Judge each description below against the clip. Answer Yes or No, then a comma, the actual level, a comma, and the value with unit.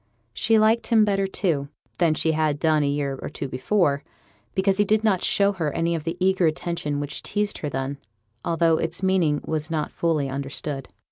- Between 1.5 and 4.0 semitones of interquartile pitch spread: No, average, 4.7 semitones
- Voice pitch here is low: No, medium, 165 Hz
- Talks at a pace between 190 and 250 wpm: Yes, average, 195 wpm